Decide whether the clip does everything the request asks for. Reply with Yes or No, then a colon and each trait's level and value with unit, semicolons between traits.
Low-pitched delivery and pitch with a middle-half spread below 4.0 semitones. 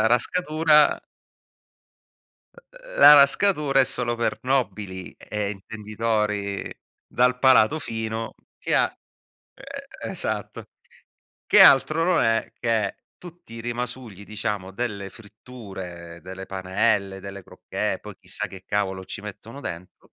No: low, 110 Hz; average, 5.1 semitones